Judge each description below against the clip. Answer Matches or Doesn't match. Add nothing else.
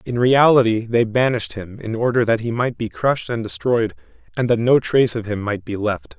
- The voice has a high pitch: Doesn't match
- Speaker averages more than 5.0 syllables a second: Matches